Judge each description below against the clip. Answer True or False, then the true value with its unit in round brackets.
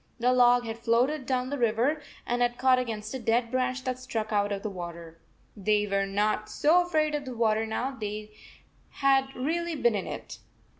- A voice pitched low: False (240 Hz)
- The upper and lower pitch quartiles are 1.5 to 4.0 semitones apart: True (3.5 semitones)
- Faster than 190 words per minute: True (200 wpm)